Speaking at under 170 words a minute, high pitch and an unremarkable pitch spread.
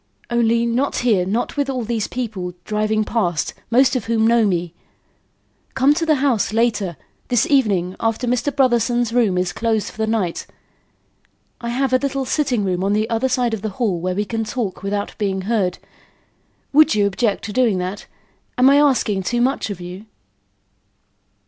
No: average, 180 wpm; high, 225 Hz; average, 3.9 semitones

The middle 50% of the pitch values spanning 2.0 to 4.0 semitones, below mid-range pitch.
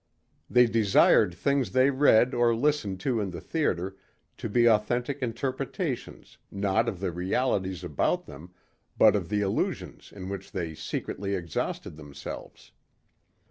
No: average, 5.1 semitones; low, 105 Hz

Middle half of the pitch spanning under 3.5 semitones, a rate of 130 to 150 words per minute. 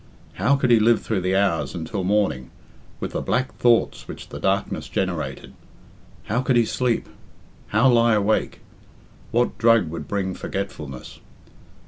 No: average, 4.0 semitones; average, 145 wpm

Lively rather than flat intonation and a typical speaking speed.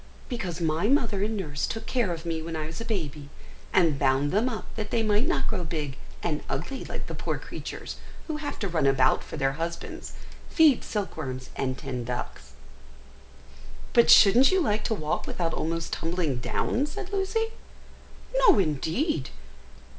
Yes: wide, 7.3 semitones; average, 170 wpm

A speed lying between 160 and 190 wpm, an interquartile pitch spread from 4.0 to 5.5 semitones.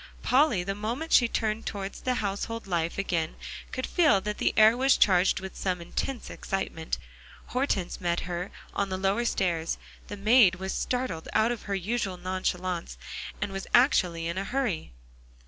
Yes: average, 165 wpm; average, 4.4 semitones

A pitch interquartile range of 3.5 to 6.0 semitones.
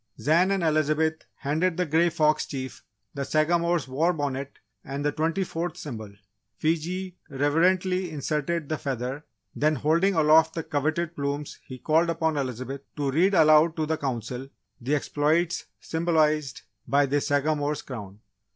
No: average, 2.8 semitones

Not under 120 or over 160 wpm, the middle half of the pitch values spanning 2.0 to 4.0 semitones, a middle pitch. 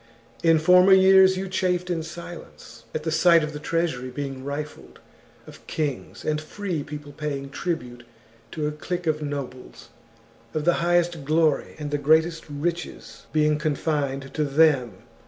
Yes: average, 155 wpm; average, 3.0 semitones; medium, 155 Hz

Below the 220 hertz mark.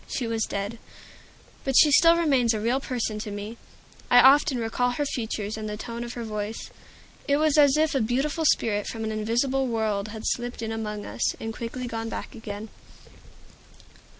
No: high, 230 Hz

